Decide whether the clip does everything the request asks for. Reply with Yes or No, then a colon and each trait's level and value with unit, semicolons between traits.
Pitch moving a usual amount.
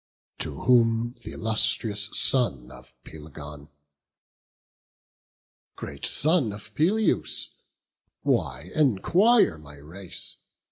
No: wide, 8.9 semitones